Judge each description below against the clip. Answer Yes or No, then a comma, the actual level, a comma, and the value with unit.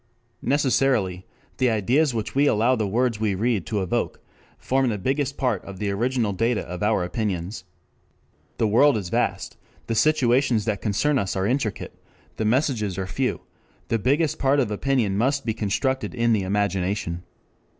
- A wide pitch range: No, average, 4.7 semitones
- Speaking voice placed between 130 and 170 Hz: No, low, 110 Hz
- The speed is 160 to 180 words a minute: Yes, average, 165 wpm